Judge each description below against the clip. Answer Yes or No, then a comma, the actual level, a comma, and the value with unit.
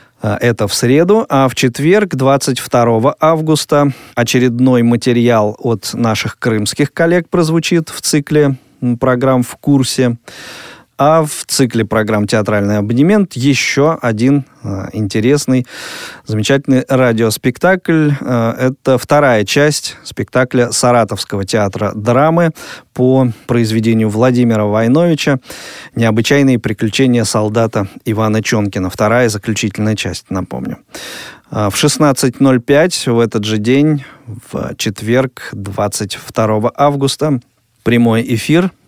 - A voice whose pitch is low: Yes, low, 125 Hz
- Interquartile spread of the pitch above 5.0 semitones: No, average, 4.2 semitones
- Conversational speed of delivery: No, slow, 100 wpm